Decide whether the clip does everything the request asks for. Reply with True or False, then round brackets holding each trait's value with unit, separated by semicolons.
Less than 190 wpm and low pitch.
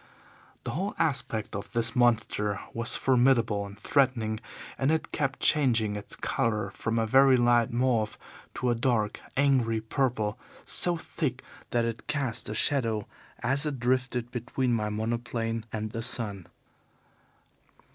True (140 wpm; 120 Hz)